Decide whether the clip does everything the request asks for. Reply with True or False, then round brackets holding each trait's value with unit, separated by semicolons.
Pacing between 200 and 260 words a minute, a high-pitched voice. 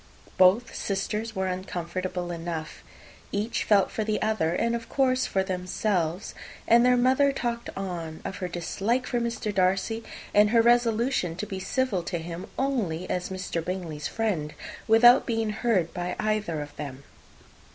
False (155 wpm; 195 Hz)